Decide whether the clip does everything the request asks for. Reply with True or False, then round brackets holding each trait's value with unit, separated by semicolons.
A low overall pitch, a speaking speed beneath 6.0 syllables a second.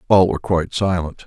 False (90 Hz; 6.4 syllables/s)